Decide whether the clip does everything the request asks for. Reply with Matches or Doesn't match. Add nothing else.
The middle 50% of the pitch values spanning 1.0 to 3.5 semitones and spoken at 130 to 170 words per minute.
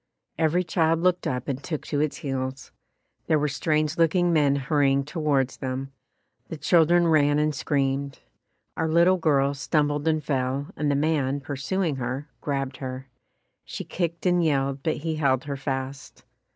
Matches